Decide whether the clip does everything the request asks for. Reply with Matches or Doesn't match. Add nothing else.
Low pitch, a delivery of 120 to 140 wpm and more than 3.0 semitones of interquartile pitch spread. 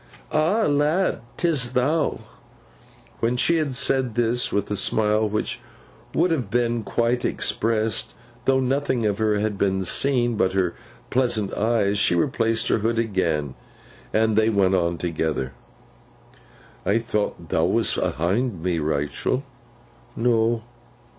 Matches